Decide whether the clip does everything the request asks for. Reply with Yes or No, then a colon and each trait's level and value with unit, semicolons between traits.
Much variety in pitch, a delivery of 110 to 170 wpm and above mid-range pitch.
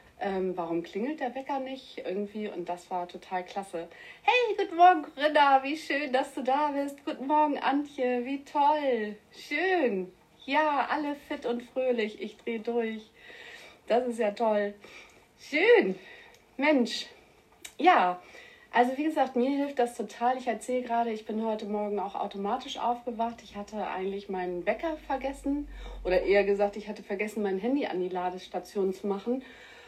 Yes: wide, 5.7 semitones; average, 160 wpm; high, 240 Hz